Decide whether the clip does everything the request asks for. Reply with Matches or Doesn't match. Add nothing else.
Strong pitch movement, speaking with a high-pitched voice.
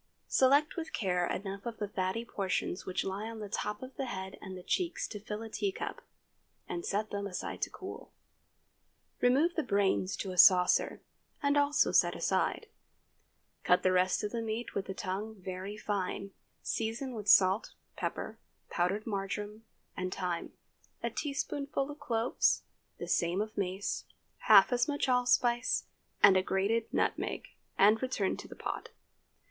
Doesn't match